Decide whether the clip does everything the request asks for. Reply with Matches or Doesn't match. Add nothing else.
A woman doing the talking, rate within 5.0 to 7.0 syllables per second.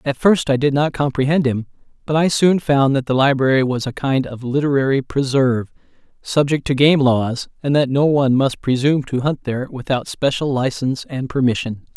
Doesn't match